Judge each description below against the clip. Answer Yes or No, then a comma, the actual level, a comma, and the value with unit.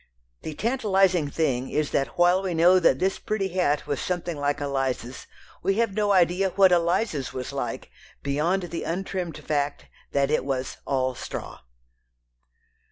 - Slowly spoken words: No, average, 155 wpm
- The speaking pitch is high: No, medium, 165 Hz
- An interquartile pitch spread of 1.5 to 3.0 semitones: No, average, 5.0 semitones